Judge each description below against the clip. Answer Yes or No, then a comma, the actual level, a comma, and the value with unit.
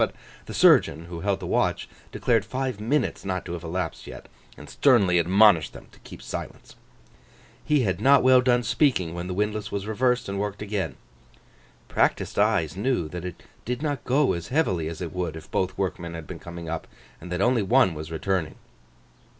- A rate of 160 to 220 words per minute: Yes, average, 190 wpm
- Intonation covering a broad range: Yes, wide, 6.1 semitones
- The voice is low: Yes, very low, 95 Hz